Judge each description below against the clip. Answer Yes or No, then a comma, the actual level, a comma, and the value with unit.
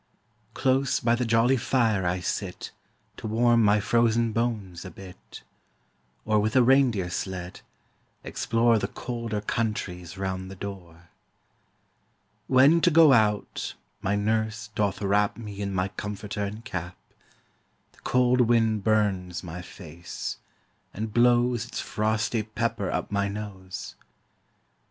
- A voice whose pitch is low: Yes, low, 105 Hz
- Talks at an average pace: No, slow, 130 wpm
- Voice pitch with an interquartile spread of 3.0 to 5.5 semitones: Yes, average, 3.3 semitones